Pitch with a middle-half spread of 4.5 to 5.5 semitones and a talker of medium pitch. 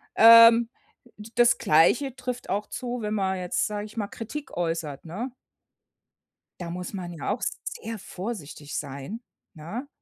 No: average, 5.2 semitones; high, 210 Hz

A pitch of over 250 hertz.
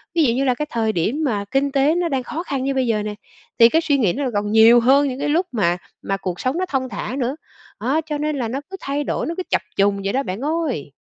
Yes: very high, 260 Hz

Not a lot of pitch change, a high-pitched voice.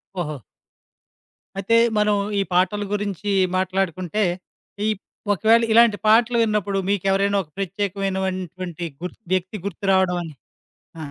Yes: narrow, 2.1 semitones; high, 195 Hz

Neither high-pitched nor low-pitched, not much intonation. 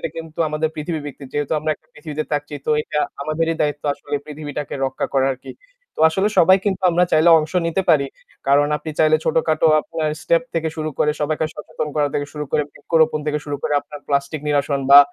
Yes: medium, 155 Hz; narrow, 1.6 semitones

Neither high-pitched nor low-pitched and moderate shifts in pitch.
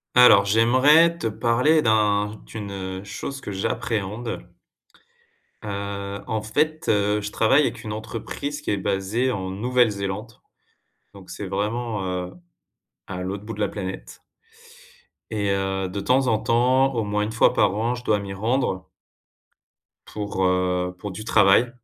No: low, 105 Hz; average, 3.3 semitones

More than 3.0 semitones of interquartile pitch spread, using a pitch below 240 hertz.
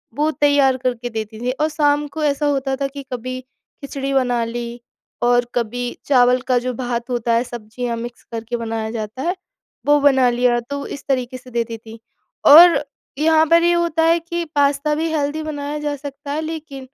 No: average, 3.4 semitones; very high, 265 Hz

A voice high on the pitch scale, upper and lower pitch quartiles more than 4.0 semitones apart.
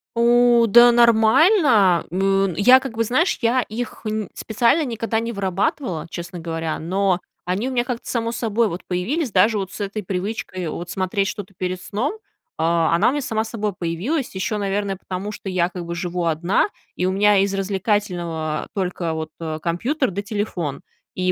Yes: high, 200 Hz; average, 4.4 semitones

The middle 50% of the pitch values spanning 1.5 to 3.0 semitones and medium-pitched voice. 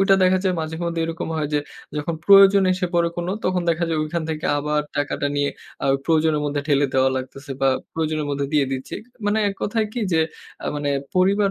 No: average, 4.0 semitones; medium, 160 Hz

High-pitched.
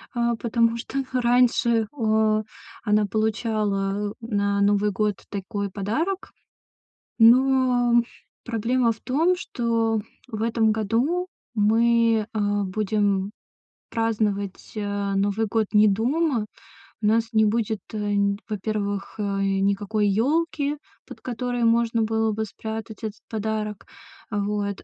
Yes: high, 220 Hz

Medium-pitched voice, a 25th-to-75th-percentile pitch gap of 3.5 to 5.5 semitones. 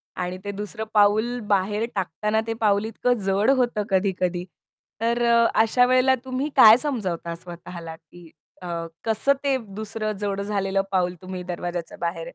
No: high, 205 Hz; average, 4.0 semitones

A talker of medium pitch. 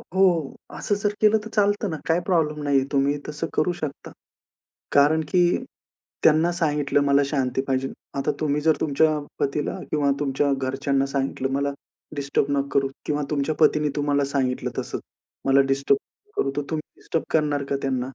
Yes: medium, 145 Hz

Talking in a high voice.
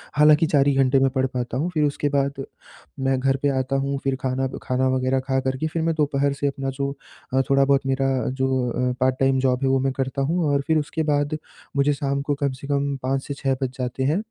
No: low, 135 Hz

